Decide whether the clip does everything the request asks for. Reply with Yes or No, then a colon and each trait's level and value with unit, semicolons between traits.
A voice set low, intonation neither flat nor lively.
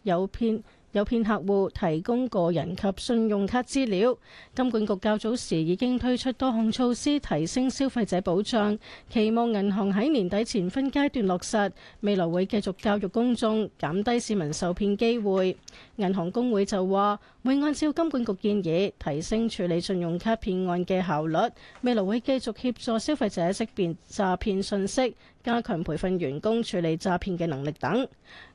No: high, 205 Hz; average, 4.2 semitones